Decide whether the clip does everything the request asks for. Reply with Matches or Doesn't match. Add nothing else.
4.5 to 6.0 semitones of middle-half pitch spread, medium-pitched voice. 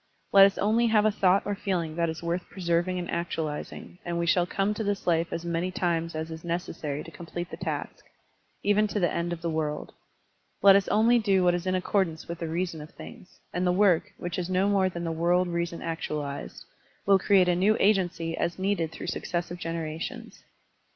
Doesn't match